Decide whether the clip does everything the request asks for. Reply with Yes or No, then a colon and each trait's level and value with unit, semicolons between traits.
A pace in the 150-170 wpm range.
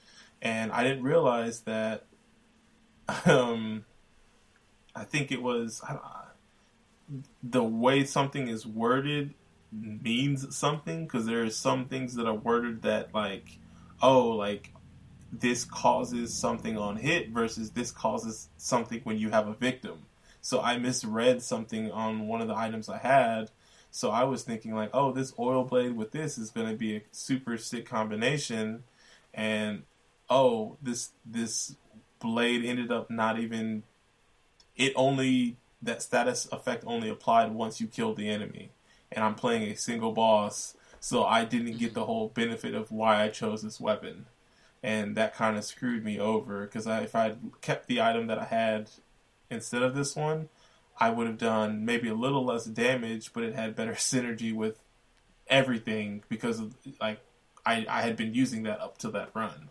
Yes: average, 165 wpm